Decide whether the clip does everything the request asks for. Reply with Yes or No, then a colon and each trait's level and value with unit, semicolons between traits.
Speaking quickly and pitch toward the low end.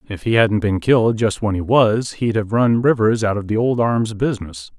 Yes: fast, 240 wpm; low, 110 Hz